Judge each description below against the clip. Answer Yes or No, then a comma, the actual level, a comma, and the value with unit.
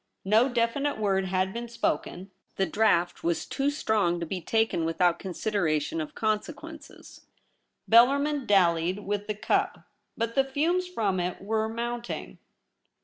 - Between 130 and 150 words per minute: Yes, average, 140 wpm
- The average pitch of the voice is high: Yes, high, 215 Hz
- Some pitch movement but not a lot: Yes, average, 4.7 semitones